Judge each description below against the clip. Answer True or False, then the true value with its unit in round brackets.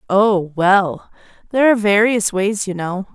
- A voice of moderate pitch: False (200 Hz)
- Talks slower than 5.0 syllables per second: True (4.4 syllables/s)